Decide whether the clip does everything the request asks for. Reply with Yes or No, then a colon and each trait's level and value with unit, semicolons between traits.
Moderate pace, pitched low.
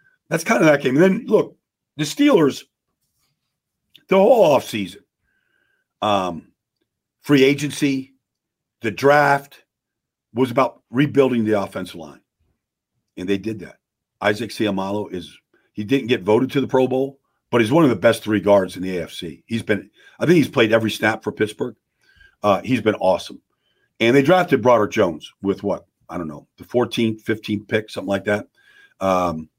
Yes: average, 165 wpm; low, 120 Hz